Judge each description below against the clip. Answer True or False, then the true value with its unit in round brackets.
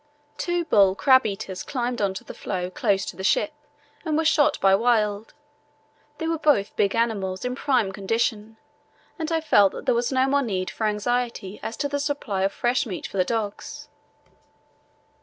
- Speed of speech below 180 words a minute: False (185 wpm)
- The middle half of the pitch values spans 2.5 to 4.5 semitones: False (5.3 semitones)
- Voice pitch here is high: True (225 Hz)